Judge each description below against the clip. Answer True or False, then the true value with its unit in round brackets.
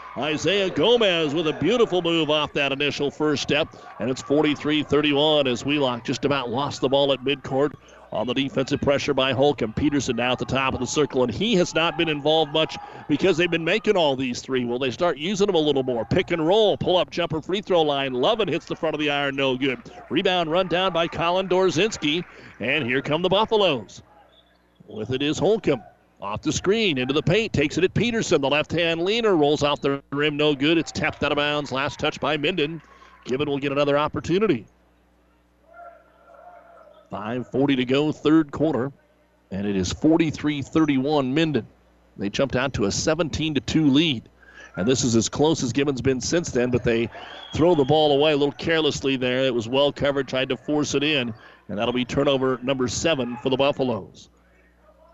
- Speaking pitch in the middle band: True (145 Hz)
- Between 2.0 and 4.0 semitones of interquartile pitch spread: True (3.6 semitones)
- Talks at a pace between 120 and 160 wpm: False (195 wpm)